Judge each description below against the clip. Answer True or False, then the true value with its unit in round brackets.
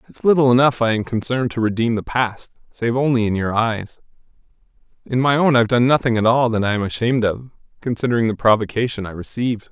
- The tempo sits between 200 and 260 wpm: True (205 wpm)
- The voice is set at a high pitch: False (115 Hz)